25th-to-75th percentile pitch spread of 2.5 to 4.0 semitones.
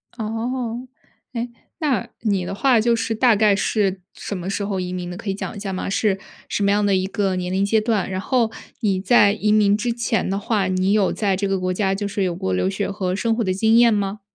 Yes: average, 2.8 semitones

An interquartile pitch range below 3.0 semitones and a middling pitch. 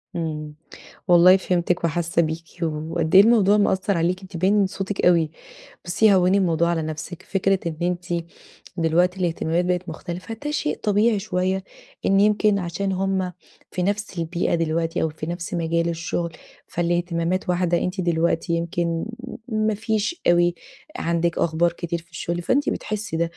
Yes: narrow, 2.4 semitones; medium, 175 Hz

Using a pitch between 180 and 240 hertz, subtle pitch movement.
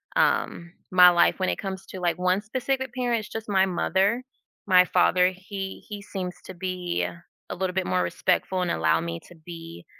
Yes: medium, 185 Hz; narrow, 2.3 semitones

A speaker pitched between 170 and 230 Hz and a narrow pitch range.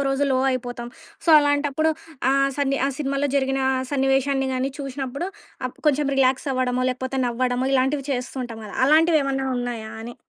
No: very high, 270 Hz; narrow, 1.7 semitones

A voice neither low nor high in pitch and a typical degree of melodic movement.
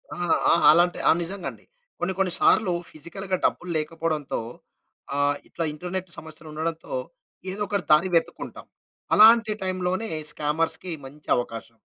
Yes: medium, 170 Hz; average, 3.4 semitones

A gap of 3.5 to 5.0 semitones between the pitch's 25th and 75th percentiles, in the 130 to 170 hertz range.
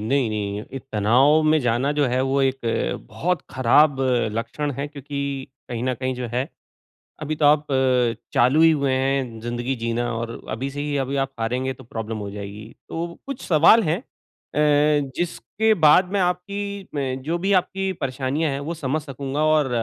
Yes: average, 4.1 semitones; low, 135 Hz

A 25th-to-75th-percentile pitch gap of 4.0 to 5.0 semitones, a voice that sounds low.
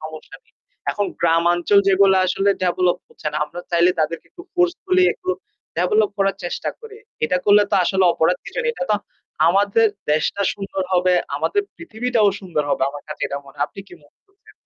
No: average, 4.4 semitones; high, 195 Hz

